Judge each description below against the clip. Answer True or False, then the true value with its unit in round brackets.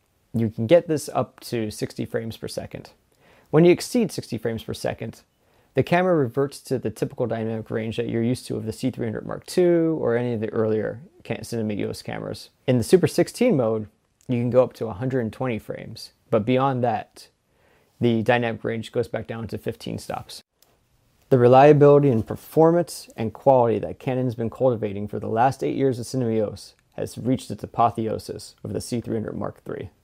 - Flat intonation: False (3.0 semitones)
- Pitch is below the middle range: True (120 Hz)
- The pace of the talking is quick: False (185 wpm)